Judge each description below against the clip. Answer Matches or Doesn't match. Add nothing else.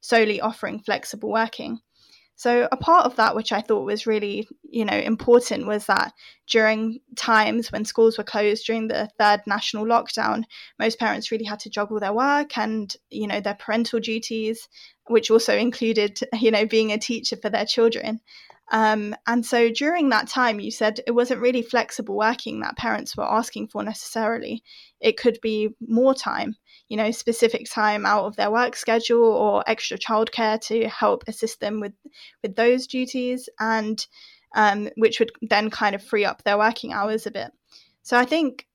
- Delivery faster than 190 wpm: Doesn't match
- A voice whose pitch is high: Matches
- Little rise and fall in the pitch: Matches